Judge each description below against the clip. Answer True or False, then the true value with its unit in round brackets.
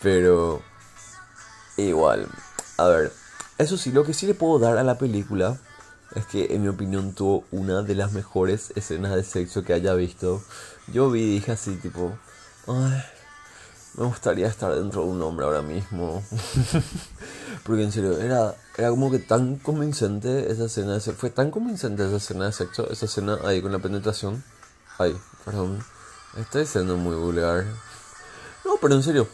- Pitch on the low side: True (105 Hz)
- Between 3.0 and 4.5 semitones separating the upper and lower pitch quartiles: False (4.9 semitones)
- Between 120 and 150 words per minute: False (170 wpm)